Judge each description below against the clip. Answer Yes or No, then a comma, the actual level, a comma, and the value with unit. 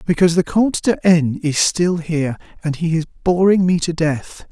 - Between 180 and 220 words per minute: Yes, average, 200 wpm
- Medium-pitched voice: Yes, medium, 165 Hz